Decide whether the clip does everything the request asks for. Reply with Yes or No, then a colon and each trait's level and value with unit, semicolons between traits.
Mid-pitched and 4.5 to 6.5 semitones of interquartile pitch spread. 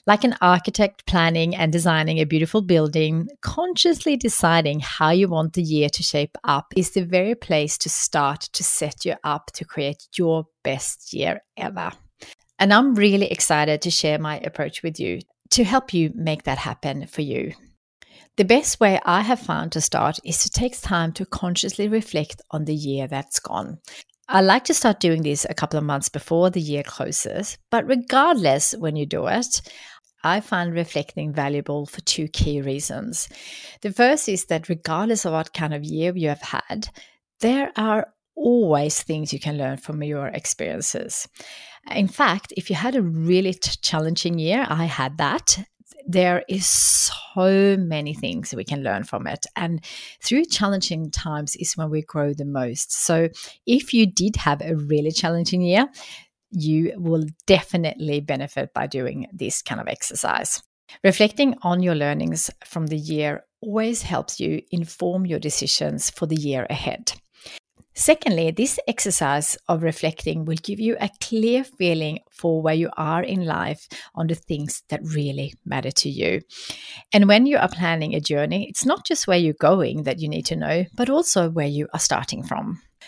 Yes: medium, 165 Hz; average, 4.9 semitones